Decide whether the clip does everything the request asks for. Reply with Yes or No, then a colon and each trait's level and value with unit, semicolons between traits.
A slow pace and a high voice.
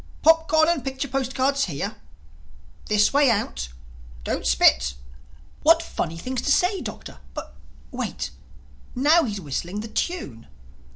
Yes: slow, 115 wpm; high, 245 Hz